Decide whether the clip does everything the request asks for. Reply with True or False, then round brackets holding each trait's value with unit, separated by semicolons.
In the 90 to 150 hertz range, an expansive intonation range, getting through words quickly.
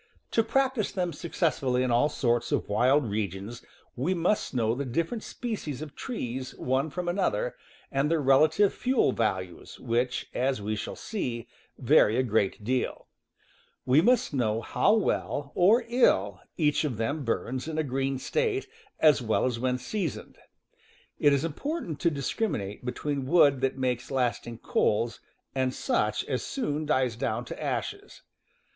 False (135 Hz; 5.8 semitones; 160 wpm)